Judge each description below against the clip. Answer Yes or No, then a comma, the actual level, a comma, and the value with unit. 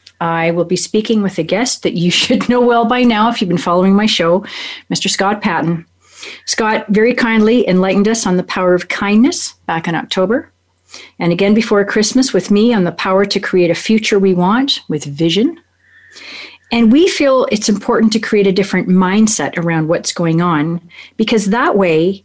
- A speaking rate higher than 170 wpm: Yes, average, 190 wpm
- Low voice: No, high, 200 Hz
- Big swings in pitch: No, average, 4.6 semitones